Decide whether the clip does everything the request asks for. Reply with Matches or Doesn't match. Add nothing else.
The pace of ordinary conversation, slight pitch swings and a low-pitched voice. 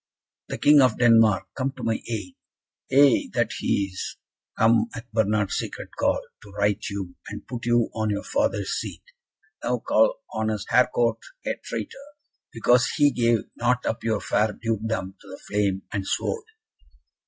Doesn't match